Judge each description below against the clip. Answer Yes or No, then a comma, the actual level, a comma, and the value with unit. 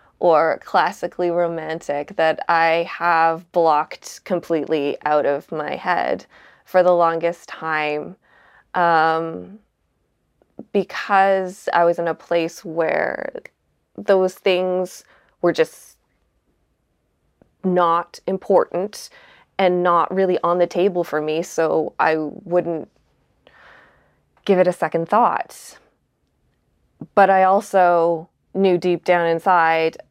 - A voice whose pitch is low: No, medium, 175 Hz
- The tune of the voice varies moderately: No, narrow, 2.3 semitones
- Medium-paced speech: No, slow, 105 wpm